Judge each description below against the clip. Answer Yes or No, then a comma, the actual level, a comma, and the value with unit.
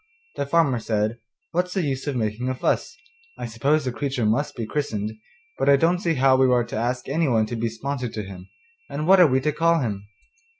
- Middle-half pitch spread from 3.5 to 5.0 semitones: Yes, average, 4.6 semitones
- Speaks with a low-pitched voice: Yes, low, 130 Hz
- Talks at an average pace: No, fast, 220 wpm